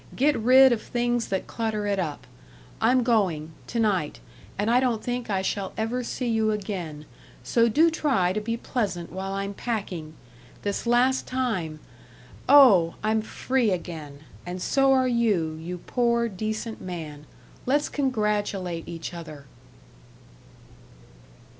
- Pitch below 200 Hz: No, high, 215 Hz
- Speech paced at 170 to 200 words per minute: No, average, 140 wpm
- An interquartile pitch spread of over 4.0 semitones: Yes, average, 5.2 semitones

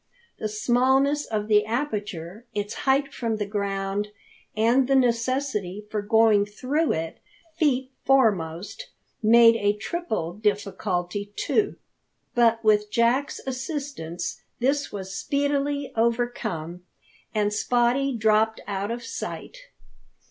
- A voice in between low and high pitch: No, high, 225 Hz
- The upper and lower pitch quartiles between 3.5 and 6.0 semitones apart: Yes, average, 4.4 semitones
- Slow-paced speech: Yes, slow, 110 wpm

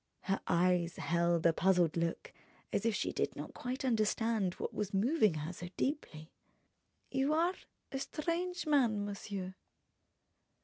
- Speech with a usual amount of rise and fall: No, wide, 7.5 semitones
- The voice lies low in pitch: No, high, 205 Hz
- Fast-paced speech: No, average, 140 wpm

